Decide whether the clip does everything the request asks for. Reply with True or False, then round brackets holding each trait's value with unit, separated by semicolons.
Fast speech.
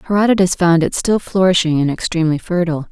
False (165 wpm)